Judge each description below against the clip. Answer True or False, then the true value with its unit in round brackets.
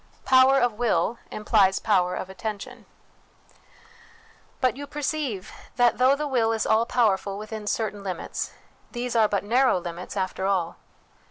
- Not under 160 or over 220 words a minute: False (150 wpm)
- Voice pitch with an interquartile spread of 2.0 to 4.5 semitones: True (4.2 semitones)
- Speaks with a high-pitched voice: True (220 Hz)